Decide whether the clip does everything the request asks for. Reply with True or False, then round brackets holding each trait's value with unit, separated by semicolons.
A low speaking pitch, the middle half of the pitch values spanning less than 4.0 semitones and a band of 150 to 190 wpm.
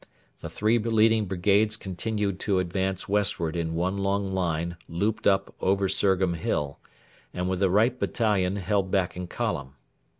True (95 Hz; 2.5 semitones; 155 wpm)